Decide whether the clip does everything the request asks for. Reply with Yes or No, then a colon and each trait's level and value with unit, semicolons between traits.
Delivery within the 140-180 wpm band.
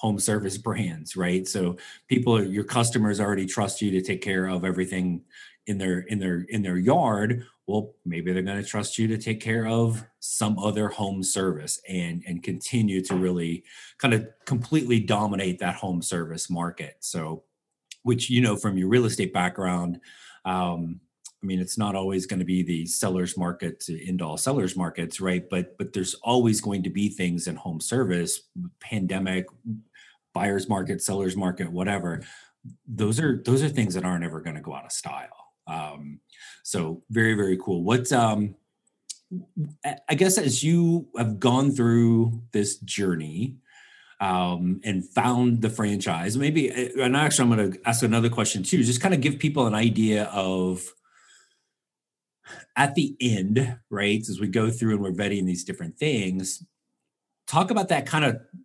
Yes: average, 170 wpm